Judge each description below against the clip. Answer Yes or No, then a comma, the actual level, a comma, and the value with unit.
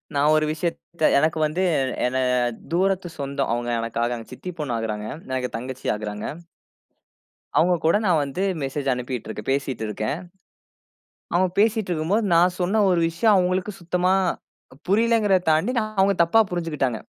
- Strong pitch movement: Yes, wide, 6.1 semitones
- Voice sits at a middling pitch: Yes, medium, 160 Hz